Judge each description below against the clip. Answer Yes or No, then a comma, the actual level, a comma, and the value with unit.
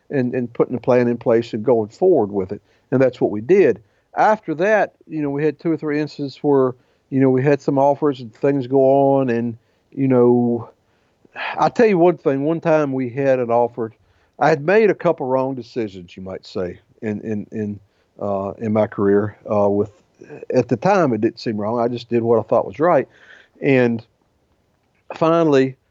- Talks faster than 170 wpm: Yes, fast, 205 wpm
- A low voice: Yes, low, 125 Hz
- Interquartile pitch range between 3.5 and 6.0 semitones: Yes, average, 4.6 semitones